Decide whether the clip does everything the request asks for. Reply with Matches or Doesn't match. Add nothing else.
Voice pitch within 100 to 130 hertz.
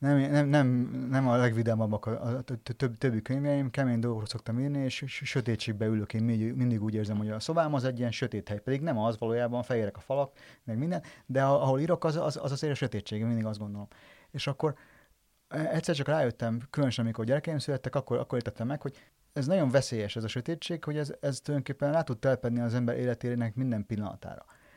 Matches